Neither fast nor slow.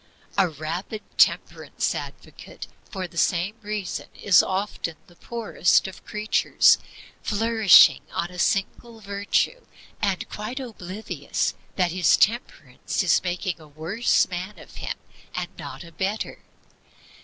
No: slow, 125 wpm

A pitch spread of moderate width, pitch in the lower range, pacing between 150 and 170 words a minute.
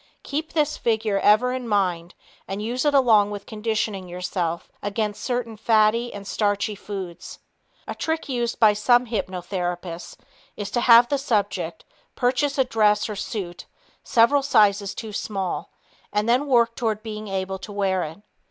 No: average, 3.3 semitones; high, 210 Hz; average, 155 wpm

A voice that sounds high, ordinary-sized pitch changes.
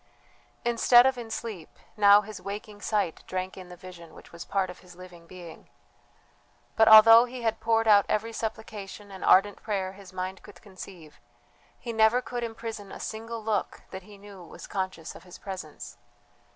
Yes: high, 205 Hz; average, 3.2 semitones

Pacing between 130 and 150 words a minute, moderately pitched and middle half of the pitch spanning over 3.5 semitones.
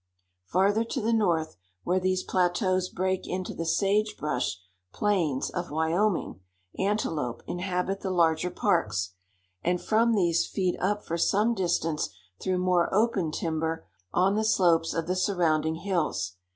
No: average, 140 wpm; medium, 180 Hz; average, 3.2 semitones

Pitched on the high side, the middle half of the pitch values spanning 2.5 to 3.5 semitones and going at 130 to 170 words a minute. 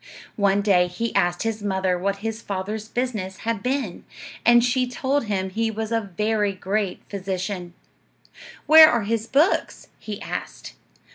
Yes: high, 210 Hz; average, 3.2 semitones; average, 150 wpm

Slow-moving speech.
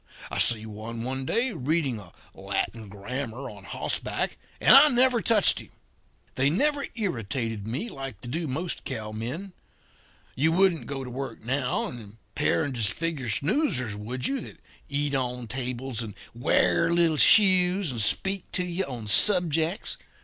No: average, 155 wpm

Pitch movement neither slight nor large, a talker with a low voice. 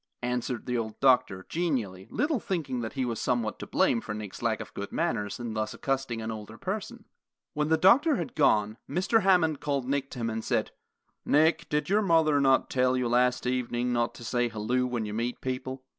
Yes: average, 4.7 semitones; low, 125 Hz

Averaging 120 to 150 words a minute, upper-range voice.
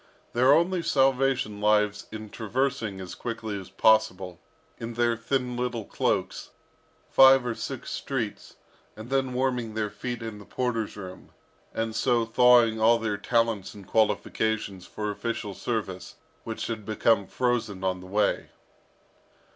No: average, 140 wpm; low, 115 Hz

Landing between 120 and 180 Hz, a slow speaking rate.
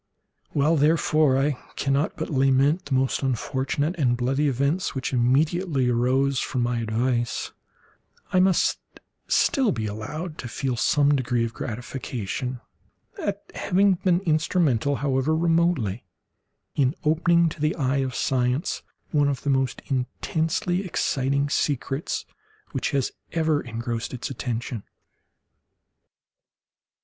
Yes: low, 135 Hz; slow, 120 wpm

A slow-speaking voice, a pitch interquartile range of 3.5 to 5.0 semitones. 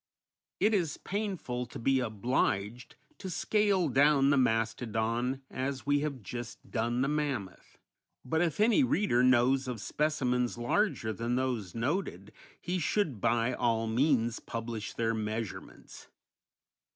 Yes: slow, 130 wpm; average, 4.5 semitones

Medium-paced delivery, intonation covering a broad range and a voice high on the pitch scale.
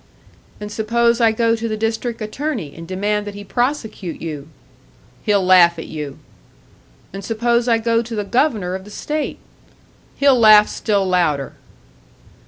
No: average, 155 wpm; average, 3.8 semitones; high, 215 Hz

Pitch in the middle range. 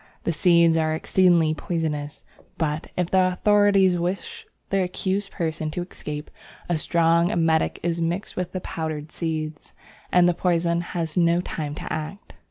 Yes: medium, 170 Hz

